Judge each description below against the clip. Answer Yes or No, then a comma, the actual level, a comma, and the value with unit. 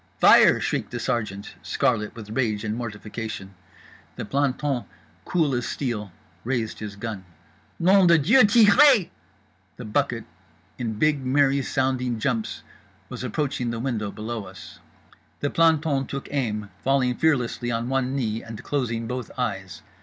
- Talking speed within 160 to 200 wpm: No, average, 140 wpm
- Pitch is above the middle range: No, low, 125 Hz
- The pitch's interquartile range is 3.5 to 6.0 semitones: Yes, average, 4.3 semitones